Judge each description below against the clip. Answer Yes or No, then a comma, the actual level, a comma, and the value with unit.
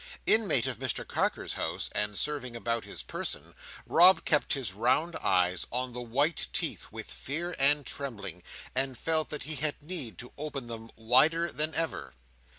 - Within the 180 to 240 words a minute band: No, average, 165 wpm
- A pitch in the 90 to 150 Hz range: Yes, low, 135 Hz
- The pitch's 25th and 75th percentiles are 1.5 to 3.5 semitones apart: No, average, 4.8 semitones